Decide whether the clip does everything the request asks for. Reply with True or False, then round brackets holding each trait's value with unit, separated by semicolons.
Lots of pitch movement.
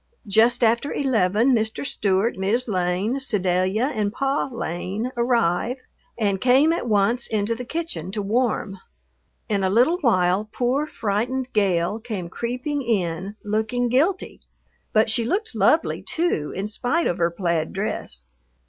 False (4.5 semitones)